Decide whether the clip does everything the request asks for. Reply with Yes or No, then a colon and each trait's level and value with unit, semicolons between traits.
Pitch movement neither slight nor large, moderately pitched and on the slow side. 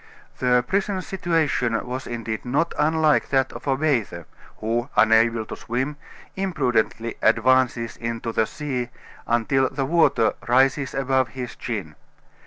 No: average, 3.7 semitones; low, 125 Hz; slow, 130 wpm